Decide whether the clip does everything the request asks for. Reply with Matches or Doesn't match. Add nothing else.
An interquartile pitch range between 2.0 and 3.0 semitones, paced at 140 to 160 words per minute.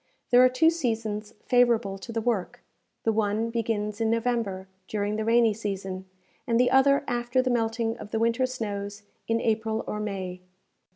Doesn't match